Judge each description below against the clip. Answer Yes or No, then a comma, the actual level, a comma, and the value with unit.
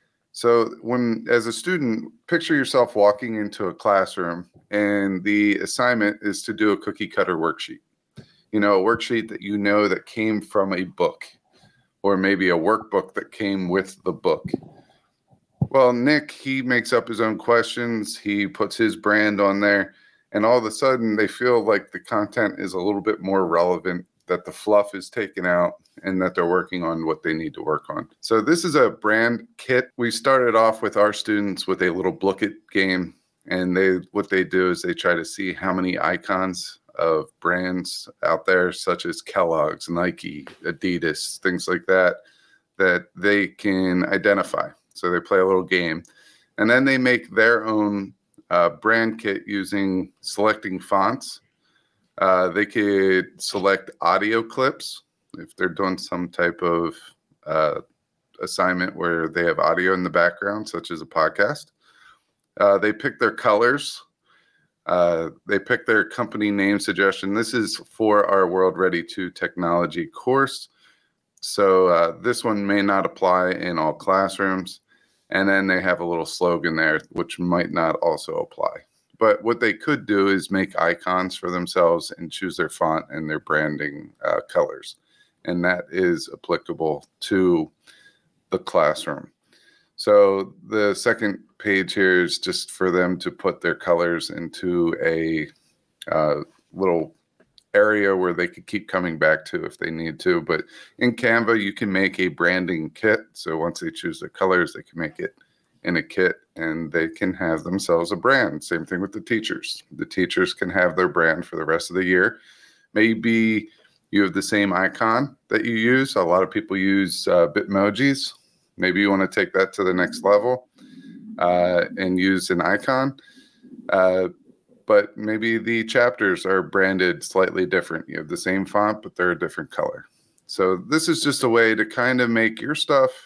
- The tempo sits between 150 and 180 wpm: Yes, average, 175 wpm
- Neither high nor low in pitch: No, low, 100 Hz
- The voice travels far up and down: No, average, 3.6 semitones